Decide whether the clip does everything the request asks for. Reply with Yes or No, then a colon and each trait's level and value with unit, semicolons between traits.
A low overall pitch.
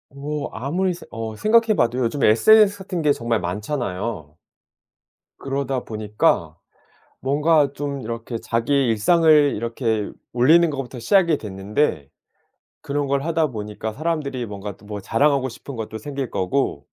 Yes: low, 130 Hz